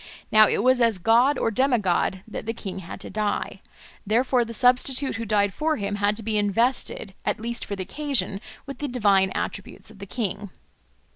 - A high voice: Yes, high, 220 Hz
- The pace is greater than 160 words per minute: Yes, average, 200 wpm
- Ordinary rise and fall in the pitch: Yes, average, 3.6 semitones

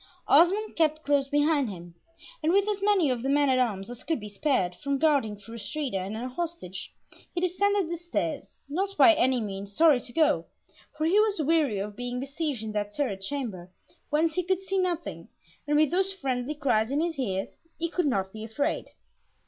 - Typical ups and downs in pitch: No, wide, 7.2 semitones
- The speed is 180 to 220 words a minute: Yes, average, 200 wpm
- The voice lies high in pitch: Yes, very high, 285 Hz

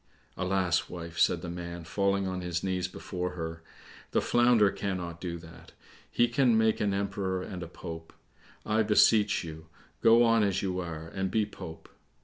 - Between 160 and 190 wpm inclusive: Yes, average, 170 wpm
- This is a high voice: No, very low, 95 Hz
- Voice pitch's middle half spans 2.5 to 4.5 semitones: Yes, average, 3.2 semitones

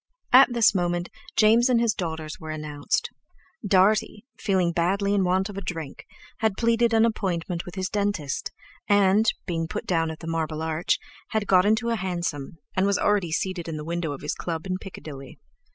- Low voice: No, medium, 185 Hz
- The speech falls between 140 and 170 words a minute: No, average, 185 wpm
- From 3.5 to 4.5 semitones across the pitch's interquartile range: Yes, average, 4.0 semitones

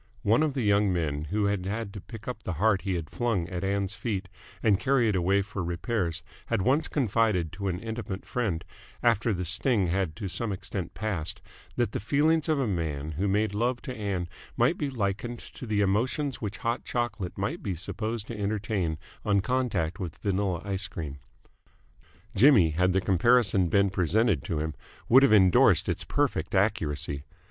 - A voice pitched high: No, low, 100 Hz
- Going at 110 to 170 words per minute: No, average, 185 wpm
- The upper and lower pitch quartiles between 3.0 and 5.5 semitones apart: Yes, average, 3.9 semitones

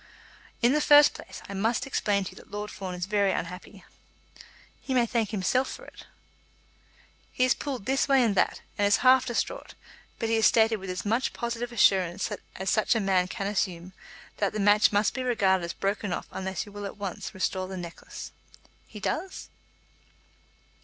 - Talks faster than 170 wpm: Yes, average, 190 wpm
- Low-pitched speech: No, high, 205 Hz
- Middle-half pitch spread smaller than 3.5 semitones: No, average, 3.9 semitones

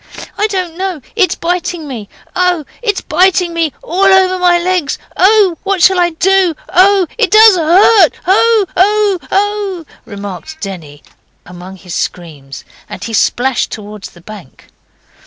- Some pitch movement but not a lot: No, wide, 8.7 semitones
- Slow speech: No, average, 145 wpm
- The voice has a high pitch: Yes, very high, 355 Hz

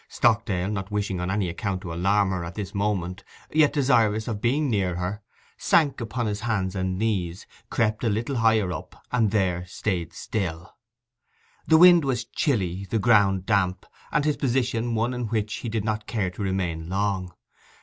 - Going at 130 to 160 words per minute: No, average, 180 wpm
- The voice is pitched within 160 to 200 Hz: No, low, 105 Hz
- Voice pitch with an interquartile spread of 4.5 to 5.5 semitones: No, average, 3.8 semitones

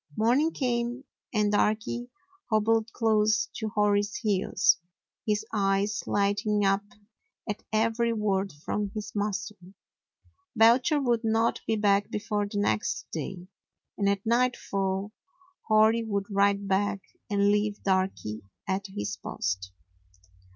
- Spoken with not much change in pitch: Yes, narrow, 2.0 semitones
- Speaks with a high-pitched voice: Yes, high, 210 Hz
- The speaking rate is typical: No, slow, 120 wpm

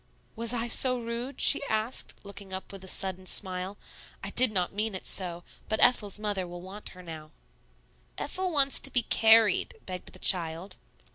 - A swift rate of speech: No, average, 180 wpm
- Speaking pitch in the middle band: No, high, 200 Hz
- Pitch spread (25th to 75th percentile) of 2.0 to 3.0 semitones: No, average, 4.0 semitones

